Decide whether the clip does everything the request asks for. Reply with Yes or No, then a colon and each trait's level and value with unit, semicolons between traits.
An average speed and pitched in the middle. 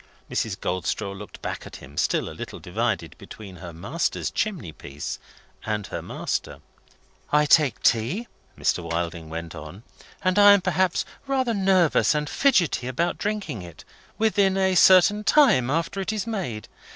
Yes: average, 155 wpm; medium, 150 Hz